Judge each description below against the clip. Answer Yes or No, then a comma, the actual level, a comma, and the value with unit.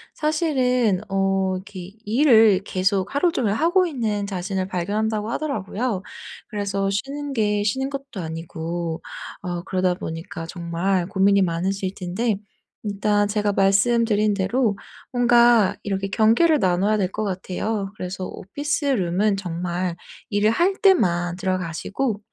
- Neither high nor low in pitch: No, high, 200 Hz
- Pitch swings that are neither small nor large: Yes, average, 3.8 semitones